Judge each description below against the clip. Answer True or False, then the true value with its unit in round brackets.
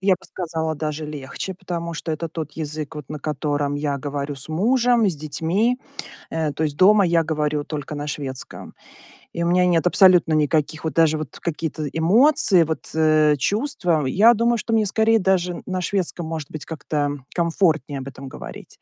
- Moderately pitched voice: True (160 Hz)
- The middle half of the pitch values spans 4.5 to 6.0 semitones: False (3.5 semitones)